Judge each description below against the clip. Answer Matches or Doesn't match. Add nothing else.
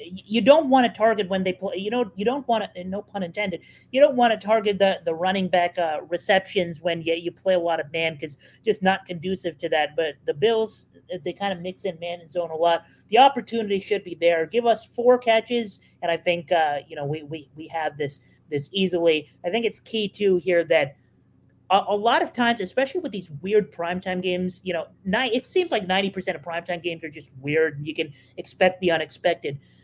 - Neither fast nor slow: Doesn't match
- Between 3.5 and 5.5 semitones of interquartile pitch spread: Matches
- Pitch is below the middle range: Doesn't match